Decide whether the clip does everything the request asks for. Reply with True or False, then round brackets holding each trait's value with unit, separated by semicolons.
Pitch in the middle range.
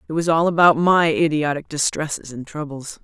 True (155 Hz)